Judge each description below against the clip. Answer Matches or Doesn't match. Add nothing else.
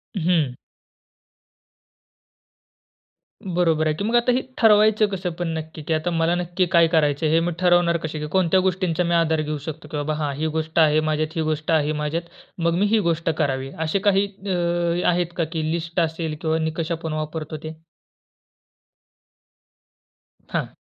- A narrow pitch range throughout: Matches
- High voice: Doesn't match